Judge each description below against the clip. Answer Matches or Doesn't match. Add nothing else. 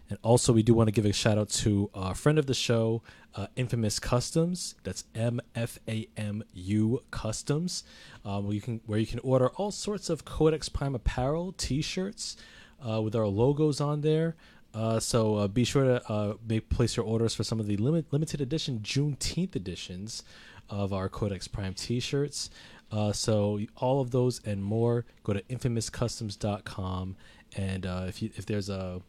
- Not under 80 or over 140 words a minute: Doesn't match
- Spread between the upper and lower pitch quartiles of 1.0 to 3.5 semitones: Doesn't match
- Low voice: Matches